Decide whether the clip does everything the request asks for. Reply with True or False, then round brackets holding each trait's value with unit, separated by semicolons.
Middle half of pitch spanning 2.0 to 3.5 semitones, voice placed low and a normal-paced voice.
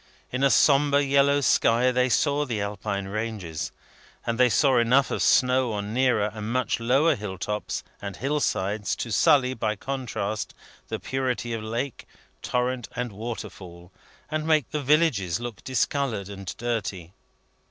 False (4.3 semitones; 120 Hz; 150 wpm)